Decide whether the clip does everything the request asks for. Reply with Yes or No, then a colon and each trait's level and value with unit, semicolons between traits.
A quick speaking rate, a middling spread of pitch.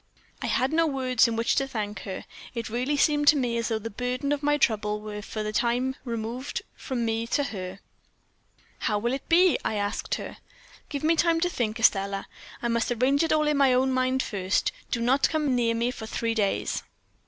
Yes: fast, 210 wpm; average, 4.0 semitones